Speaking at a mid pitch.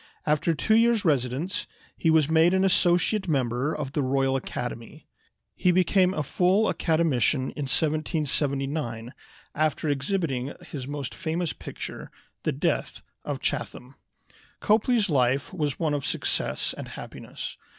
Yes: medium, 150 Hz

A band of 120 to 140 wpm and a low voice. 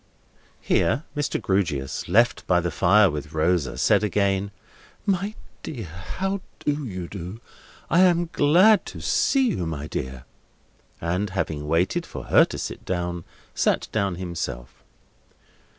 Yes: slow, 135 wpm; very low, 95 Hz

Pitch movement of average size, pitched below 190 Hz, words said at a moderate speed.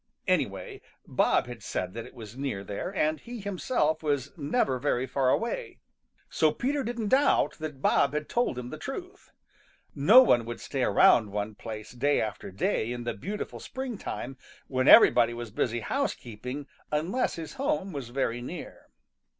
No: wide, 8.9 semitones; medium, 140 Hz; average, 165 wpm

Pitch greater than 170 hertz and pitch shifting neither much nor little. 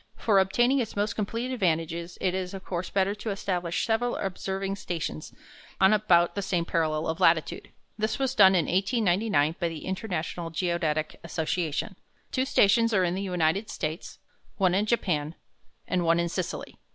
Yes: medium, 185 Hz; average, 3.5 semitones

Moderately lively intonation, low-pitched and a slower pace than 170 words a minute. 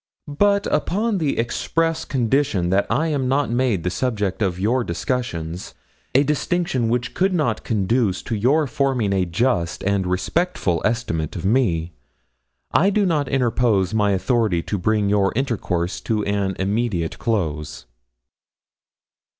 No: wide, 6.0 semitones; low, 115 Hz; average, 140 wpm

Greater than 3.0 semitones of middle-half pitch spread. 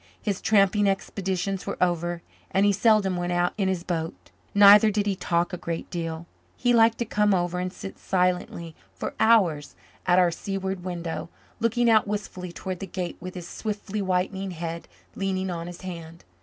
No: narrow, 2.6 semitones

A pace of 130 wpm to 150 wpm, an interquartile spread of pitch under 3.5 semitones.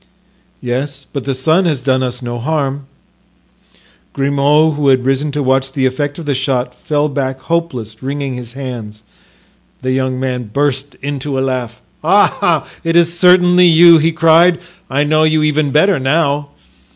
No: average, 165 wpm; average, 3.1 semitones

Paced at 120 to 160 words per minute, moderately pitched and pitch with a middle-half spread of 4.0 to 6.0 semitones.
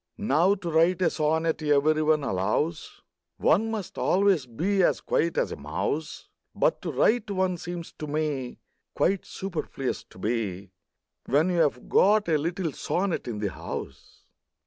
Yes: average, 155 wpm; medium, 160 Hz; average, 5.0 semitones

